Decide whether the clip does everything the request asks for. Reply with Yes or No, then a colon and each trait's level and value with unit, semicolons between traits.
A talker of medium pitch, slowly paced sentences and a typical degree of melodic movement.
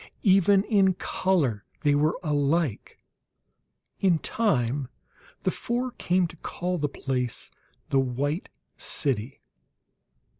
No: medium, 155 Hz; slow, 105 wpm; wide, 5.7 semitones